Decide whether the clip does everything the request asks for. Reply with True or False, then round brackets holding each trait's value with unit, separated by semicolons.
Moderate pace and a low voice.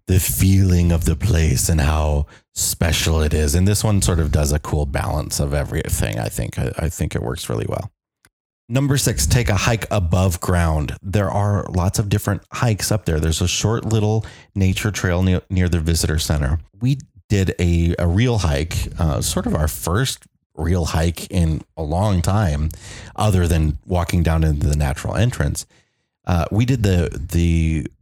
True (180 wpm; 90 Hz)